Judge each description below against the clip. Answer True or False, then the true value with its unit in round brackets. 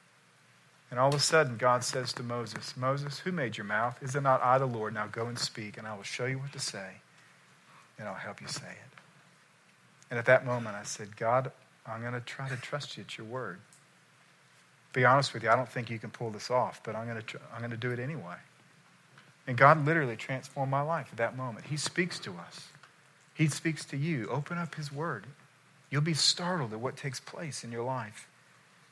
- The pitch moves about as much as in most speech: True (4.0 semitones)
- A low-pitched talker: True (130 Hz)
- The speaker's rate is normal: False (220 wpm)